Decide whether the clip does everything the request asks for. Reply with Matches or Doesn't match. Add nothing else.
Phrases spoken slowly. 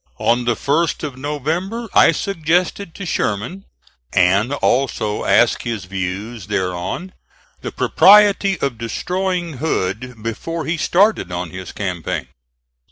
Matches